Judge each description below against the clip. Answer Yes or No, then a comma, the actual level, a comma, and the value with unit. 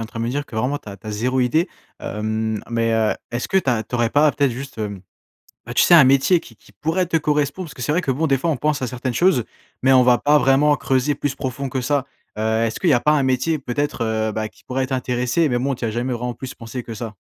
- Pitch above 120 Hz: Yes, low, 130 Hz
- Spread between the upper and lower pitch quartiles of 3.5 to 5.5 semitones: Yes, average, 3.9 semitones